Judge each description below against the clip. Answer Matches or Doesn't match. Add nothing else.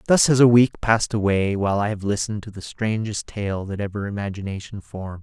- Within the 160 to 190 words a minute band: Doesn't match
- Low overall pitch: Matches